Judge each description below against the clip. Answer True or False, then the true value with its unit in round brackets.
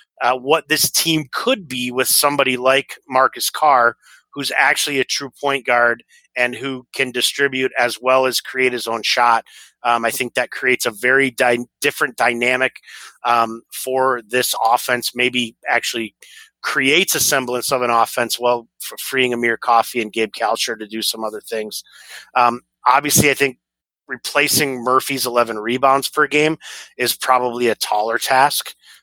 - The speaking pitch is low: True (125 Hz)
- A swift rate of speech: False (160 wpm)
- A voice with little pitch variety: True (2.0 semitones)